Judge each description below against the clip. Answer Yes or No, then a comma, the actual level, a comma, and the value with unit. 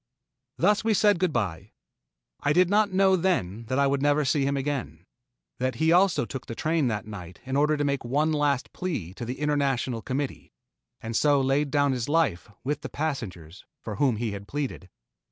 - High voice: No, medium, 140 Hz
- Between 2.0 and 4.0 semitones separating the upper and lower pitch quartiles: No, average, 4.8 semitones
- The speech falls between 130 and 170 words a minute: No, average, 195 wpm